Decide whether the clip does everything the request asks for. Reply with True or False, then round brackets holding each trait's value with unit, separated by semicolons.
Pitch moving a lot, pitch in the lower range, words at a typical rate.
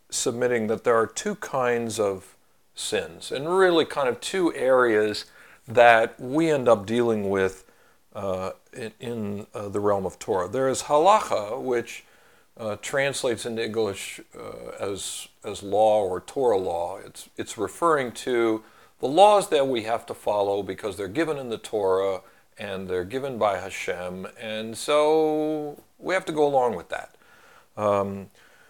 True (6.2 semitones; 115 Hz; 155 wpm)